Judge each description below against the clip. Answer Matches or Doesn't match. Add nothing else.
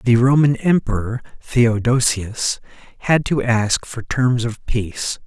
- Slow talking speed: Matches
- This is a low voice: Matches